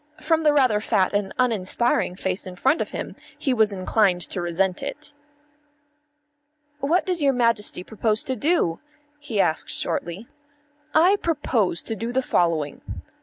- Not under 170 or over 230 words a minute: No, average, 150 wpm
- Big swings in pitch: Yes, wide, 7.1 semitones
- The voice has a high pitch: Yes, high, 220 Hz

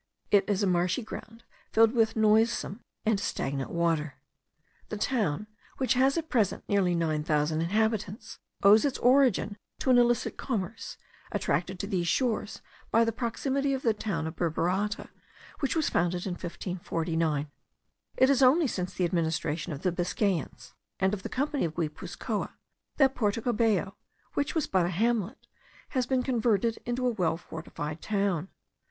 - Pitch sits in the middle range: No, high, 205 Hz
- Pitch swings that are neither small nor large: No, wide, 5.7 semitones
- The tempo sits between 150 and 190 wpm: Yes, average, 160 wpm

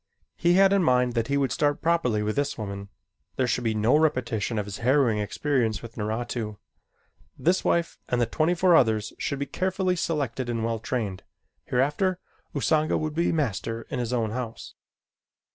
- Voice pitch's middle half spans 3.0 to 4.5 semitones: No, wide, 5.6 semitones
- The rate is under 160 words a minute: No, average, 180 wpm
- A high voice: No, low, 125 Hz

